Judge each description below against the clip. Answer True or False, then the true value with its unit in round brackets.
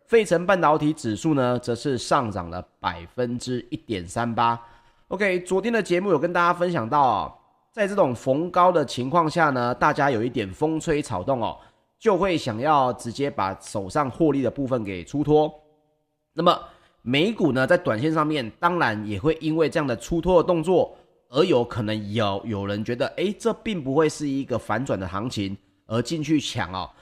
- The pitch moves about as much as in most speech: False (5.8 semitones)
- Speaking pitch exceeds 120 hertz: True (140 Hz)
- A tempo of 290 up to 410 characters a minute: False (275 characters per minute)